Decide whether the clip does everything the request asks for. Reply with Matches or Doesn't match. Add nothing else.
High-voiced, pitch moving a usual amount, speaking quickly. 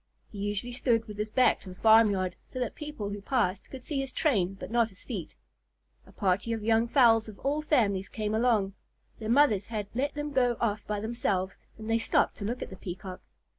Matches